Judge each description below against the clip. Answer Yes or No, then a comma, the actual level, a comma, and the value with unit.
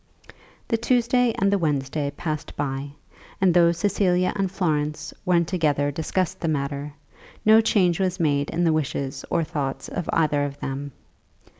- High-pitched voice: No, medium, 160 Hz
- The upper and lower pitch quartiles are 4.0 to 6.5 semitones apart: Yes, average, 4.3 semitones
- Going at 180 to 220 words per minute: No, average, 155 wpm